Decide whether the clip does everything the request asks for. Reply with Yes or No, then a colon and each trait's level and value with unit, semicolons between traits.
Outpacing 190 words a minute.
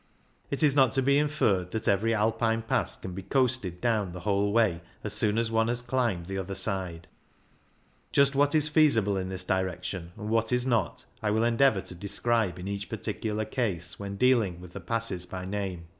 Yes: average, 200 wpm